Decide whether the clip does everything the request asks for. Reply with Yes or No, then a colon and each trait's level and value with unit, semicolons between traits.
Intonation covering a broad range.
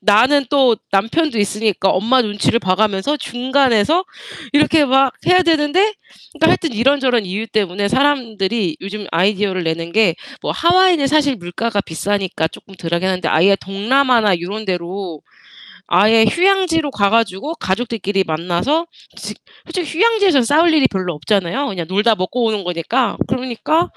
Yes: wide, 6.7 semitones